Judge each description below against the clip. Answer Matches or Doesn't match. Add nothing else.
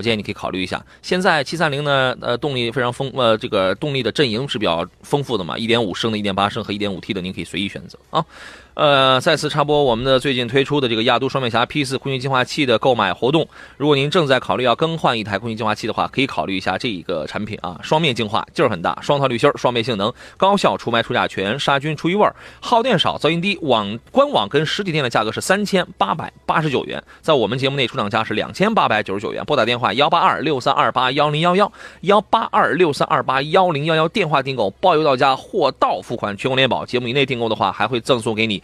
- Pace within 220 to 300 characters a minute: Doesn't match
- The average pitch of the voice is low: Matches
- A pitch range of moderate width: Matches